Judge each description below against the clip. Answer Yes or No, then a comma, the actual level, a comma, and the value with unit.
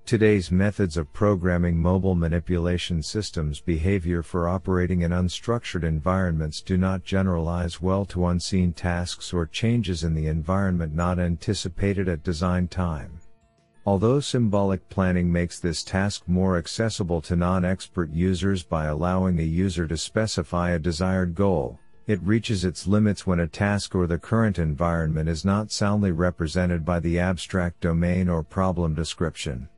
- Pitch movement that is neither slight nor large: No, narrow, 2.2 semitones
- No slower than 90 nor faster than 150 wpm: Yes, average, 145 wpm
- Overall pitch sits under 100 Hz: Yes, very low, 90 Hz